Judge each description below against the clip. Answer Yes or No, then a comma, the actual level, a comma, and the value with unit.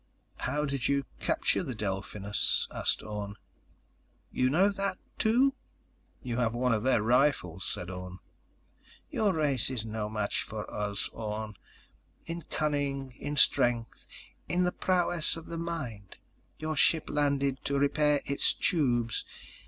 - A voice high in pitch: No, low, 130 Hz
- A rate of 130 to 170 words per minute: Yes, slow, 135 wpm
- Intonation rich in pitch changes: Yes, wide, 5.9 semitones